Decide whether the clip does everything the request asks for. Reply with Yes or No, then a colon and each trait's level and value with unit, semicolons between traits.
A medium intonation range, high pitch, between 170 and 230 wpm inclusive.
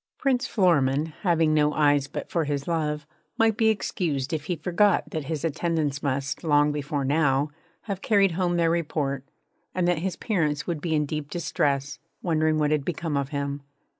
No: average, 3.3 semitones; medium, 155 Hz; average, 180 wpm